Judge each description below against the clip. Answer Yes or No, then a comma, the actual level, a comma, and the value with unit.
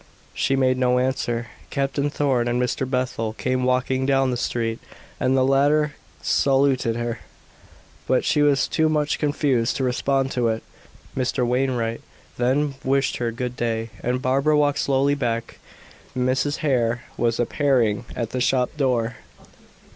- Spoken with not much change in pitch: Yes, narrow, 2.3 semitones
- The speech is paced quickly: No, average, 145 wpm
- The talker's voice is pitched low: Yes, low, 130 Hz